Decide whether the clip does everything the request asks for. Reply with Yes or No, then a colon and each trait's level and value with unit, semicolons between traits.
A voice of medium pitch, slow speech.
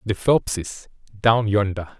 No: low, 105 Hz; slow, 120 wpm